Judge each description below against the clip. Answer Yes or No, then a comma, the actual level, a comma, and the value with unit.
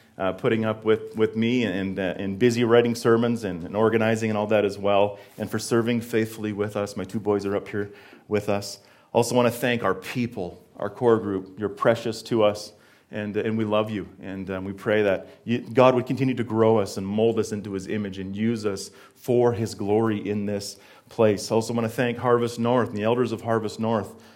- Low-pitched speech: Yes, low, 110 Hz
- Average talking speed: No, fast, 225 wpm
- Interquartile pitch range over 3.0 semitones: No, narrow, 2.4 semitones